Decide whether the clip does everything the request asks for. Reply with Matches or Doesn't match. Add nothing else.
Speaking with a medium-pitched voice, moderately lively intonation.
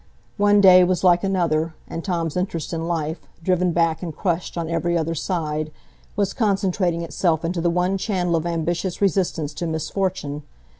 Doesn't match